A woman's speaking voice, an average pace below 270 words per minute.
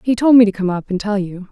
No: female; fast, 355 wpm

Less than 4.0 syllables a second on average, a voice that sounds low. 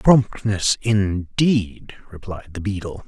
Yes: 3.3 syllables/s; low, 100 Hz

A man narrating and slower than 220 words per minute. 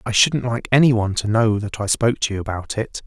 No: male; fast, 255 wpm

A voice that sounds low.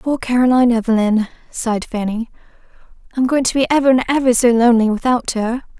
No: high, 240 Hz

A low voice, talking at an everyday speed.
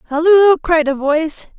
No: very high, 320 Hz; average, 150 wpm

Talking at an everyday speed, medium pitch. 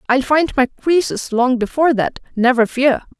No: average, 170 wpm; very high, 265 Hz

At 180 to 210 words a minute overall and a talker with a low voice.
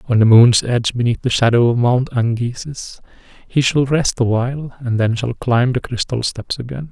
Yes: average, 190 wpm; low, 125 Hz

